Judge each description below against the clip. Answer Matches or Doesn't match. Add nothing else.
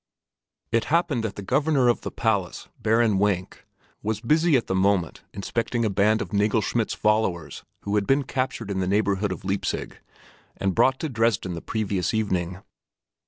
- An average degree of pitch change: Matches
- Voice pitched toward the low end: Matches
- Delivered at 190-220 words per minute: Doesn't match